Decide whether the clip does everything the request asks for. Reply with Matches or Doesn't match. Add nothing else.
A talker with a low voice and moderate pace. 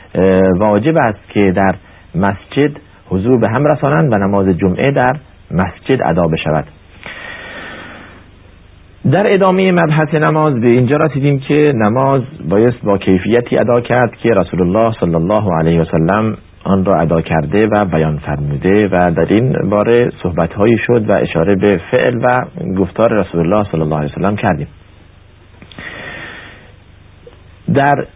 Matches